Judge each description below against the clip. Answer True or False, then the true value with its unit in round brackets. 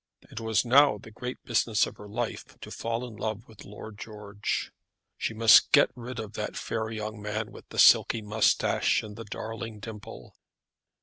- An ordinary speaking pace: True (180 wpm)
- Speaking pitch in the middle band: False (110 Hz)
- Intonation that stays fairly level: True (1.5 semitones)